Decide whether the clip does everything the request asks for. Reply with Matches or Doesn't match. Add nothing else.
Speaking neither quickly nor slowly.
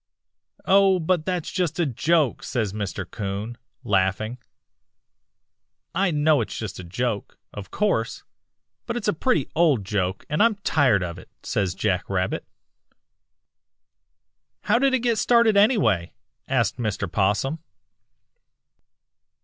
Doesn't match